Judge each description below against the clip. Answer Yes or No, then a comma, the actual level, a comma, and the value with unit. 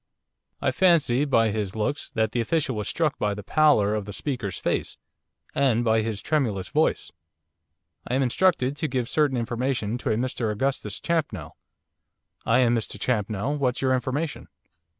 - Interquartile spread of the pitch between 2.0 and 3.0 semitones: No, average, 4.4 semitones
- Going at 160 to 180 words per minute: Yes, average, 165 wpm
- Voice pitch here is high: No, low, 125 Hz